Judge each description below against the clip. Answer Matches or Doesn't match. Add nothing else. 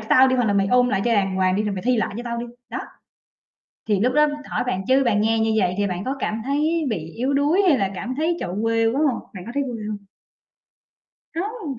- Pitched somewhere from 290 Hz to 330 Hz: Doesn't match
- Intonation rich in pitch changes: Doesn't match